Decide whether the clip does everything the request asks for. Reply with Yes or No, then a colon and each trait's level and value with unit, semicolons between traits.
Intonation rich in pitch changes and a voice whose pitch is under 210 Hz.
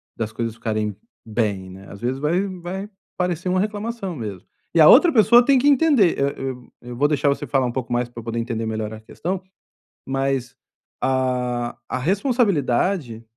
Yes: wide, 8.0 semitones; low, 135 Hz